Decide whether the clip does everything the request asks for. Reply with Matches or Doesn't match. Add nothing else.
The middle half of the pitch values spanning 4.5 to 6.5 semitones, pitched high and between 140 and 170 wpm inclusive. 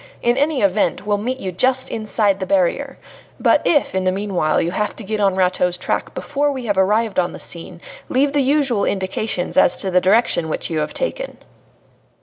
Doesn't match